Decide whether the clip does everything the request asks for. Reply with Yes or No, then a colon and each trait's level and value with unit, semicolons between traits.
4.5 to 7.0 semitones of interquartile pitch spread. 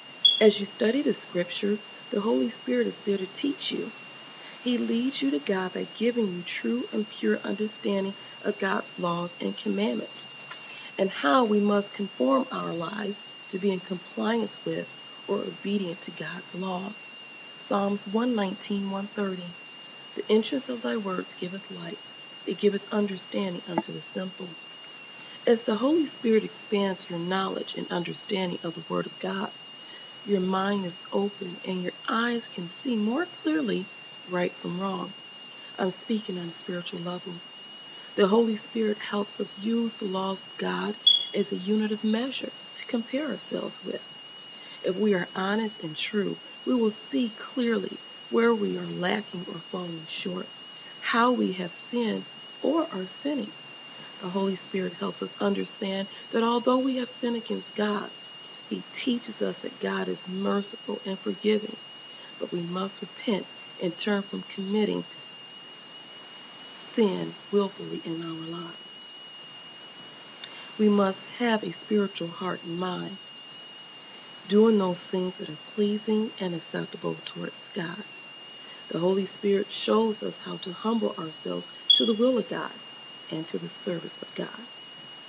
No: average, 3.3 semitones